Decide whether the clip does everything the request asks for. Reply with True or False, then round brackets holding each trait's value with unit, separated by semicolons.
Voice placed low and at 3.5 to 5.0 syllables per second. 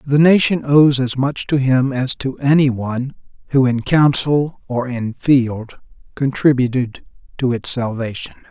True (130 Hz; 4.2 syllables/s)